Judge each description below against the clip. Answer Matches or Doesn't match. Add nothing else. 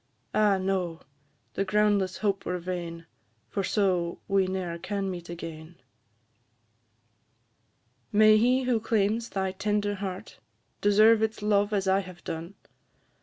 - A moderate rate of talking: Doesn't match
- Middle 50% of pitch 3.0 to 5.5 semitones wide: Doesn't match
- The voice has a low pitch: Doesn't match